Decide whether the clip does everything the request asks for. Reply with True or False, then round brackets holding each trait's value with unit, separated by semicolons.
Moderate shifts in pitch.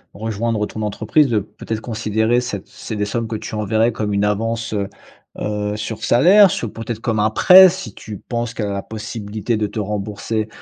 False (1.9 semitones)